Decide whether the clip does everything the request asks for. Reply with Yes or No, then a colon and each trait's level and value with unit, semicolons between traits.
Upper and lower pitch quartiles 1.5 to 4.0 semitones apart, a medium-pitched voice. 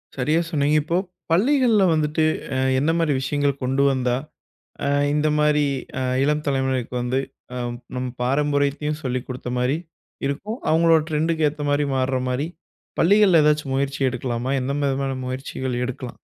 Yes: average, 2.8 semitones; medium, 145 Hz